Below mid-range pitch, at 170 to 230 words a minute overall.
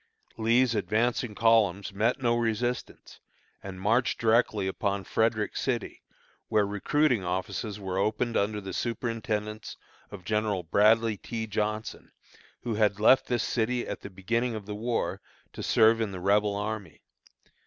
No: low, 110 Hz; average, 145 wpm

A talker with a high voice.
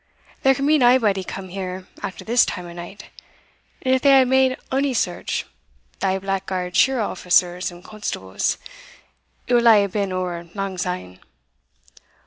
Yes: high, 195 Hz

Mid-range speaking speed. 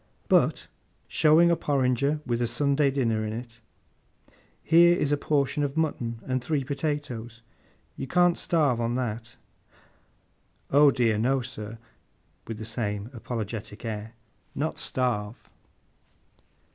No: slow, 125 wpm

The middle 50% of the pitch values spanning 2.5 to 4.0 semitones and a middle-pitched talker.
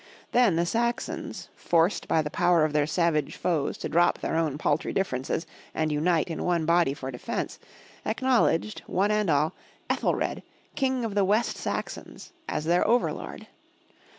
No: average, 5.2 semitones; medium, 170 Hz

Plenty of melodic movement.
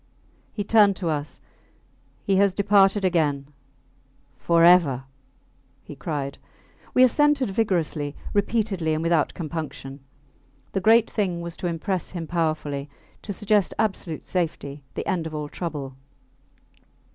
No: average, 4.7 semitones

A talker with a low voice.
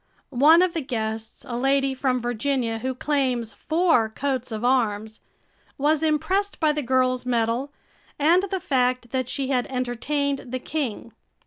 No: very high, 260 Hz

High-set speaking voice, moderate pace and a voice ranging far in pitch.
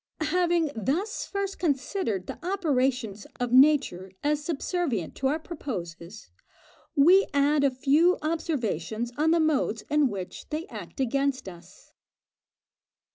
No: very high, 280 Hz; slow, 125 wpm; wide, 6.1 semitones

